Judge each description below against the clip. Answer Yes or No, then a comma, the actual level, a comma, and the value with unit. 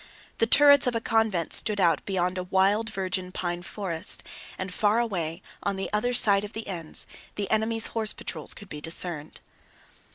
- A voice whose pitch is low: No, high, 195 Hz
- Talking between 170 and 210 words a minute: Yes, average, 175 wpm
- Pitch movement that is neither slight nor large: Yes, average, 3.7 semitones